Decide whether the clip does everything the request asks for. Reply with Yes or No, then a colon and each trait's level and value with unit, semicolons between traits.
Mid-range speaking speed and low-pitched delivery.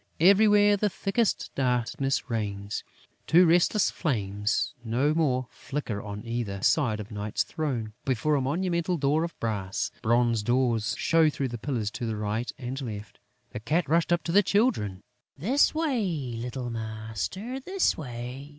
Yes: average, 150 wpm; low, 130 Hz